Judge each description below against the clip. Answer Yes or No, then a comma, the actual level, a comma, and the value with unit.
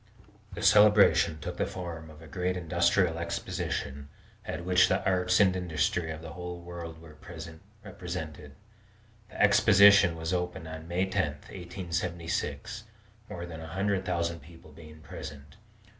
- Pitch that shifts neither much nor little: No, narrow, 2.3 semitones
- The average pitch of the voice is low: Yes, very low, 85 Hz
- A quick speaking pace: No, average, 145 wpm